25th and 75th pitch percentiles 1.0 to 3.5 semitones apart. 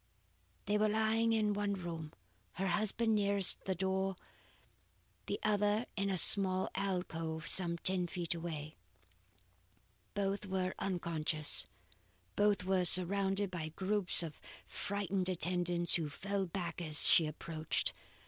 Yes: average, 2.9 semitones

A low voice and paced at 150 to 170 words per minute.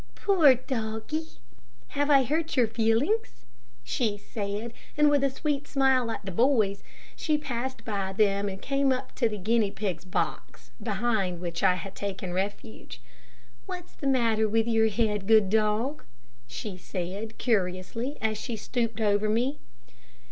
No: high, 220 Hz; average, 155 wpm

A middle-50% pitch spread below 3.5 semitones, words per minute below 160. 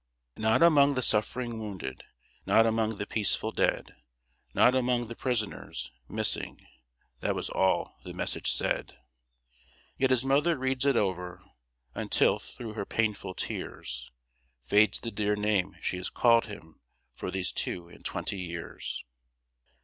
No: average, 4.6 semitones; average, 140 wpm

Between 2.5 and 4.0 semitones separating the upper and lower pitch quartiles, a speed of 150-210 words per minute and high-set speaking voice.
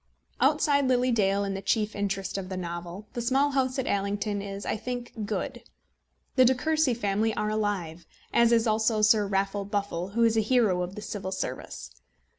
Yes: average, 3.4 semitones; average, 190 wpm; high, 210 Hz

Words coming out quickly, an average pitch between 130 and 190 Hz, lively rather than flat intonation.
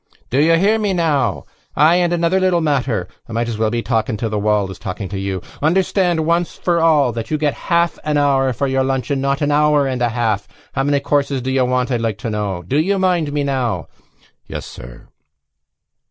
Yes: fast, 225 wpm; low, 135 Hz; wide, 5.7 semitones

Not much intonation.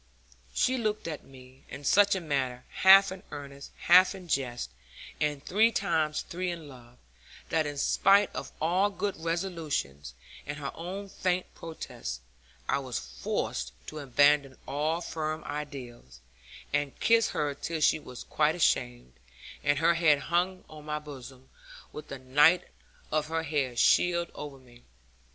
No: average, 4.3 semitones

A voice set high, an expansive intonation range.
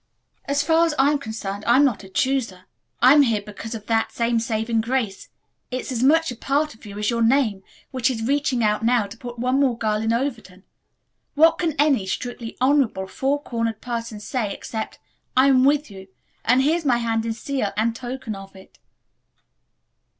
No: high, 235 Hz; average, 3.8 semitones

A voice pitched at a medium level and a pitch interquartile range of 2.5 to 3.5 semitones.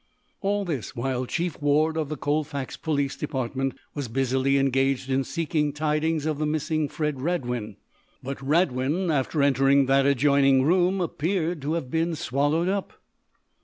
Yes: medium, 145 Hz; average, 2.9 semitones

